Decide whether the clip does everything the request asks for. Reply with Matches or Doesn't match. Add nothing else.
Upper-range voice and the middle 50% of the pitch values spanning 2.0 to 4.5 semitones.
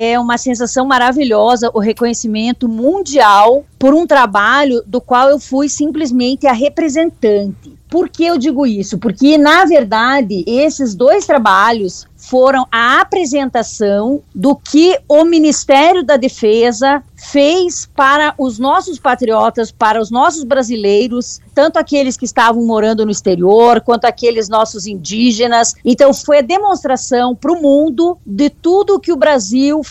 Matches